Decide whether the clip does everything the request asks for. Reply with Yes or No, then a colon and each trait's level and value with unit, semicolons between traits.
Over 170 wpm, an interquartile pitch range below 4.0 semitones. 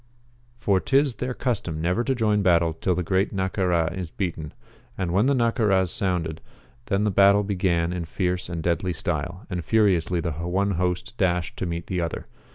Yes: average, 180 wpm; average, 3.0 semitones